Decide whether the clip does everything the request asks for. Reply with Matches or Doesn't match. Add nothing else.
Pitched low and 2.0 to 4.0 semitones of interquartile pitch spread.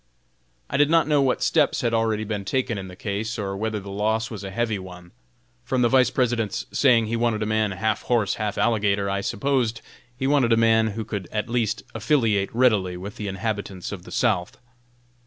Matches